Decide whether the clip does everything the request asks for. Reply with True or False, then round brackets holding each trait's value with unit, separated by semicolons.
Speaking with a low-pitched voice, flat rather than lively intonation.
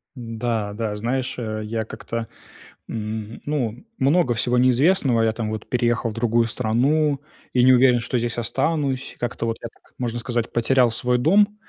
True (120 Hz; 2.3 semitones)